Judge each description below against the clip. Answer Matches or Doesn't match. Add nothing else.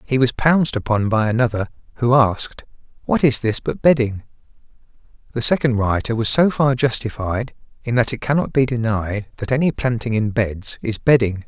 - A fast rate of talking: Doesn't match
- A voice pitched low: Matches